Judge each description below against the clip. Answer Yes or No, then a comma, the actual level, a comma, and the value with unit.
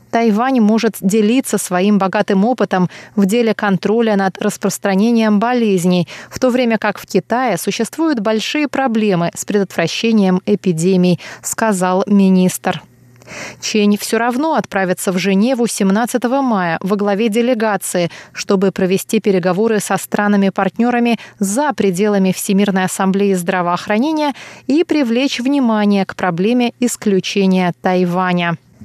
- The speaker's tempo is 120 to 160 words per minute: No, slow, 110 wpm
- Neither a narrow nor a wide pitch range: Yes, average, 3.4 semitones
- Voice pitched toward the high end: Yes, high, 205 Hz